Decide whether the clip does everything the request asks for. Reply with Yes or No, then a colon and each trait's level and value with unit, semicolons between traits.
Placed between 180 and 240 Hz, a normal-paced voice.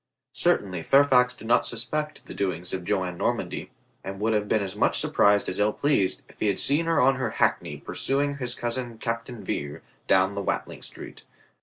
No: low, 110 Hz; average, 190 wpm